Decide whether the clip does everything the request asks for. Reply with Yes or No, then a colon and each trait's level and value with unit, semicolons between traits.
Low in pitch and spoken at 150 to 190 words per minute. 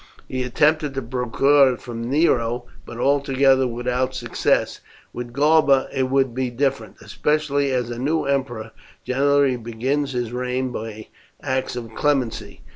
No: low, 130 Hz; average, 140 wpm